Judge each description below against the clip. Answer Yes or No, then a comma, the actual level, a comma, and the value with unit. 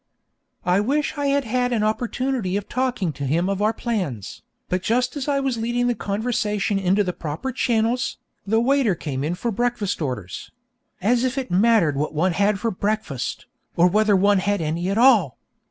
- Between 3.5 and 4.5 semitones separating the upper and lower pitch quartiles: No, average, 5.2 semitones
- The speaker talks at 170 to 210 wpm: Yes, average, 185 wpm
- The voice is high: Yes, high, 210 Hz